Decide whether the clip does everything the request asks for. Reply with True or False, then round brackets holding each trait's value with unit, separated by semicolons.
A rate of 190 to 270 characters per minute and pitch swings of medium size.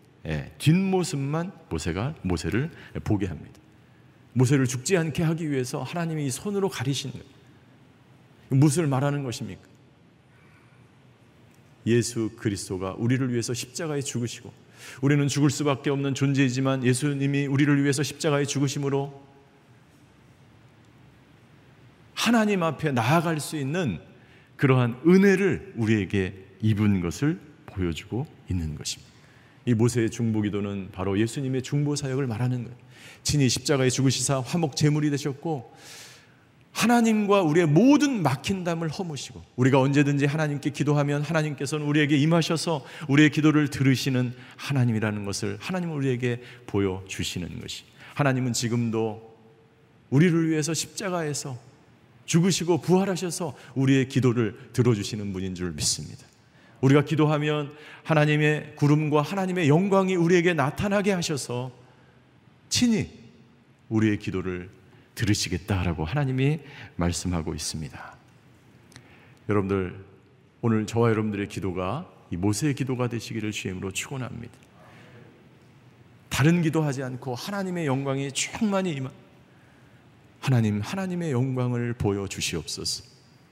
False (315 characters per minute; 4.1 semitones)